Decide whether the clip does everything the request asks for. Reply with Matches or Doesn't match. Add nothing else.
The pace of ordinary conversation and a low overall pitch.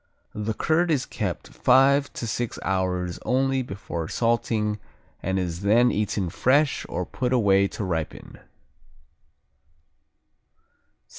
Doesn't match